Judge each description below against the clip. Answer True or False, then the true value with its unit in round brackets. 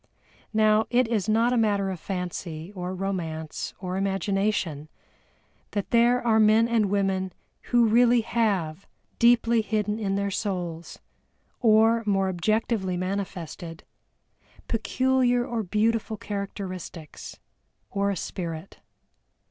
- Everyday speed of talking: False (115 wpm)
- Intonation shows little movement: False (3.5 semitones)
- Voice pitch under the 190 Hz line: False (200 Hz)